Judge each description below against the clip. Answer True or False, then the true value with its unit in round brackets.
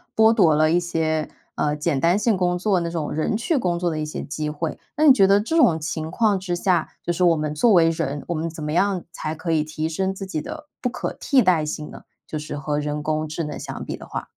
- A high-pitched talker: False (165 Hz)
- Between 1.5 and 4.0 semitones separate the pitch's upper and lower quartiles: True (3.7 semitones)